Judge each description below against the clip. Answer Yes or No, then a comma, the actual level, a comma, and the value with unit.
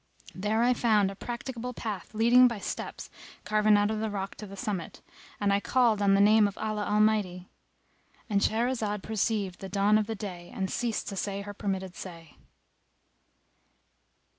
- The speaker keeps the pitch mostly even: Yes, narrow, 2.0 semitones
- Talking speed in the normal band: Yes, average, 165 wpm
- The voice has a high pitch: Yes, high, 210 Hz